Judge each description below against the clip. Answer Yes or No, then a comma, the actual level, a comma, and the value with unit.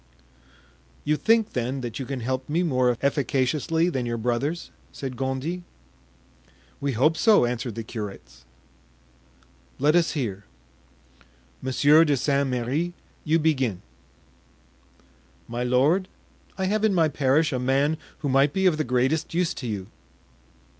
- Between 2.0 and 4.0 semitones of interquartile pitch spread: No, average, 4.4 semitones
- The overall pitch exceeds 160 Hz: No, low, 135 Hz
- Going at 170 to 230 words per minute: No, average, 140 wpm